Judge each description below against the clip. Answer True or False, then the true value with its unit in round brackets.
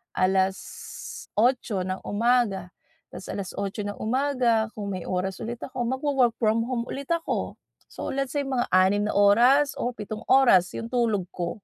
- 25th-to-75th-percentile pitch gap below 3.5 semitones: False (4.3 semitones)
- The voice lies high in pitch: True (225 Hz)